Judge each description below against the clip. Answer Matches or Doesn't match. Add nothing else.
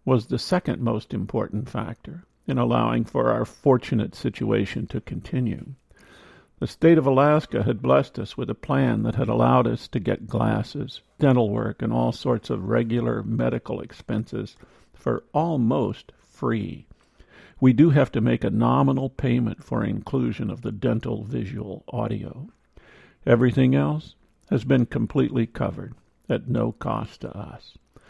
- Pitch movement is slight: Doesn't match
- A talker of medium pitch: Doesn't match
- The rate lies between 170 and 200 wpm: Doesn't match